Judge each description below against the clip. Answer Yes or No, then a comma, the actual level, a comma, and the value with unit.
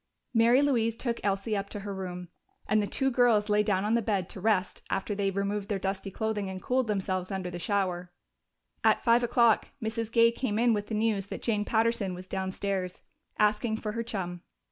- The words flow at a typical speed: No, fast, 210 wpm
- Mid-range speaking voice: No, high, 210 Hz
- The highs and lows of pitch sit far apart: No, average, 2.9 semitones